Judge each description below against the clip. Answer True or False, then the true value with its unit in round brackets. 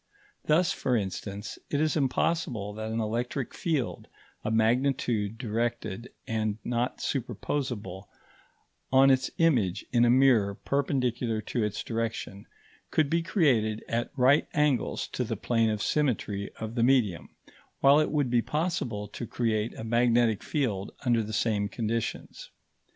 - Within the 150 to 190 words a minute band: False (140 wpm)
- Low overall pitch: True (120 Hz)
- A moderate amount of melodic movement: True (3.8 semitones)